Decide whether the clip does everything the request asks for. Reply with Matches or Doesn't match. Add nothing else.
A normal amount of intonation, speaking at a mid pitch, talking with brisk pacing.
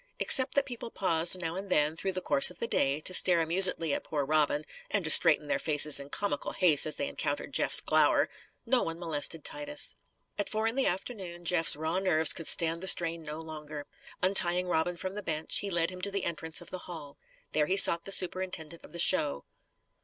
Matches